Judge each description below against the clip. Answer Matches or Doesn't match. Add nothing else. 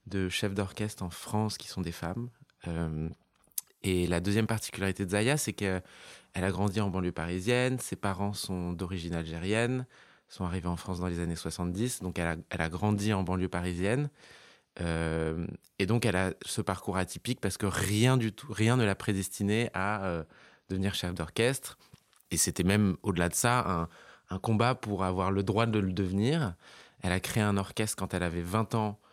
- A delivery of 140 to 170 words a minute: Doesn't match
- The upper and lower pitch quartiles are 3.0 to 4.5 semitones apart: Matches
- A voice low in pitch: Matches